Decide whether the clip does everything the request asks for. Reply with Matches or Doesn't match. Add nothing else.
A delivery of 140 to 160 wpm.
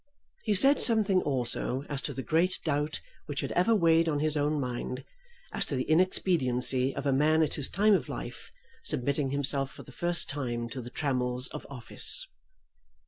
Doesn't match